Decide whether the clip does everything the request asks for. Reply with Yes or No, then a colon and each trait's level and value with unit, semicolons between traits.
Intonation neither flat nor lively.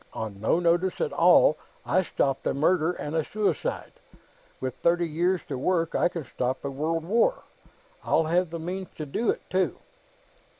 Yes: average, 3.4 semitones